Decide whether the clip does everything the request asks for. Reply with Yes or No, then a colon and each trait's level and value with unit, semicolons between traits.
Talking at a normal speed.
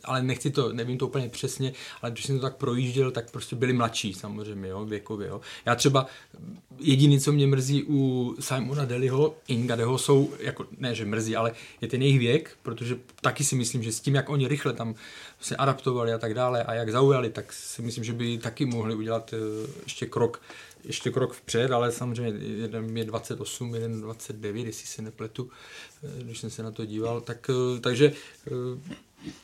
No: fast, 185 wpm